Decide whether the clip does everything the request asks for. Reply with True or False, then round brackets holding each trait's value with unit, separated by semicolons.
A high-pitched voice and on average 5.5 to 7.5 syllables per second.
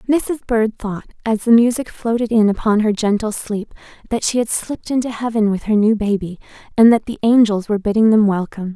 True (220 Hz; 5.8 syllables/s)